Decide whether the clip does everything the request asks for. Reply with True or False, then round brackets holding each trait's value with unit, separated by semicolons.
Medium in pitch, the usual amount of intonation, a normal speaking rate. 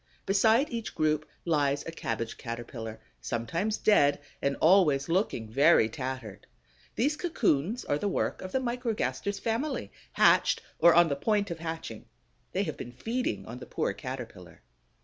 False (165 Hz; 8.3 semitones; 150 wpm)